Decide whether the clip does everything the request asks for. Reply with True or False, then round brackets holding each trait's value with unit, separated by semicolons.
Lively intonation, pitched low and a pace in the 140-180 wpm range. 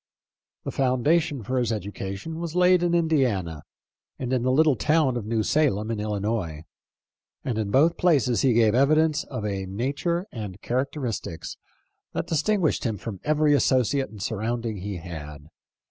True (6.5 semitones; 125 Hz; 155 wpm)